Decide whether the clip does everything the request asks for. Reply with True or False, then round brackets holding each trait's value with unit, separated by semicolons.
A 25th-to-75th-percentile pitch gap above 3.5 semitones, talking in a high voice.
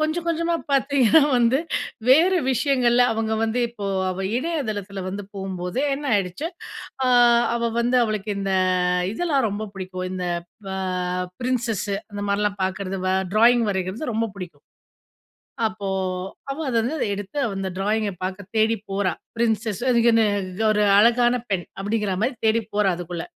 True (4.0 semitones; 220 Hz)